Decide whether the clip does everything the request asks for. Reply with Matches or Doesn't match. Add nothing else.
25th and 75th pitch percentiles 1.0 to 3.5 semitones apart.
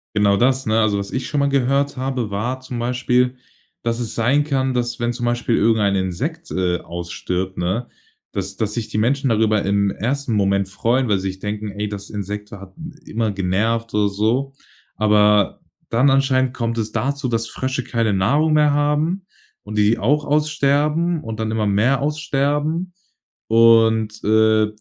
Doesn't match